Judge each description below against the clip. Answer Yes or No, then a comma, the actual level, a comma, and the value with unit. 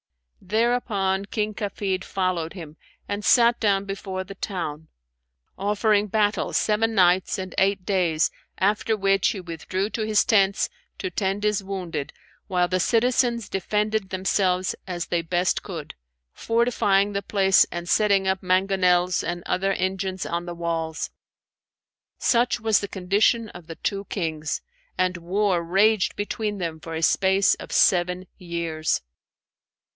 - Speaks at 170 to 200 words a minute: No, average, 140 wpm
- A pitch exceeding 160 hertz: Yes, high, 190 Hz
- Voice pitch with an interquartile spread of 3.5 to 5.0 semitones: No, narrow, 2.6 semitones